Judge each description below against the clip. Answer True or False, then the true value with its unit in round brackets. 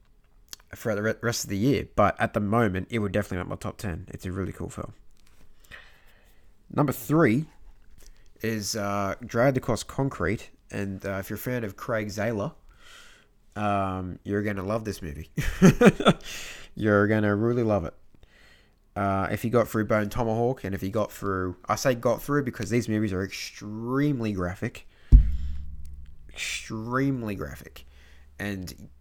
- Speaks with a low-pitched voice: True (105 Hz)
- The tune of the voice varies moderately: True (3.3 semitones)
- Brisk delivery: False (155 wpm)